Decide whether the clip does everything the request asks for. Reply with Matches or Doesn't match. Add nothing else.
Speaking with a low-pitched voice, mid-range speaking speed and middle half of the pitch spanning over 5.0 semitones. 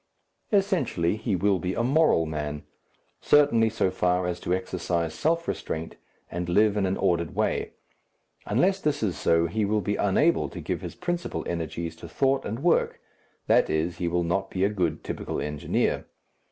Matches